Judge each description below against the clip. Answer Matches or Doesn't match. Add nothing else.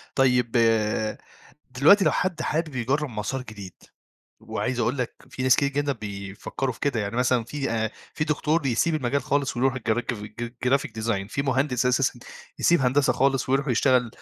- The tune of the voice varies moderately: Matches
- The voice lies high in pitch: Doesn't match